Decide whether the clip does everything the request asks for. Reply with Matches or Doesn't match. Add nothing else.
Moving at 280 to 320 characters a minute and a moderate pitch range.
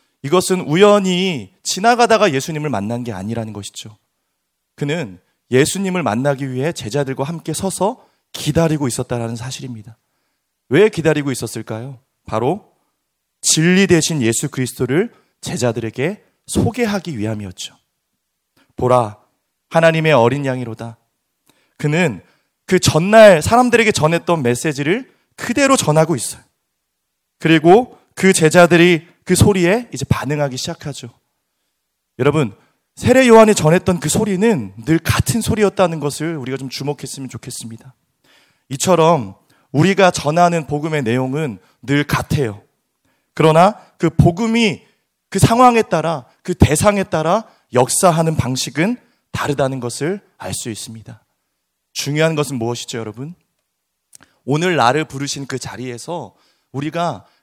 Doesn't match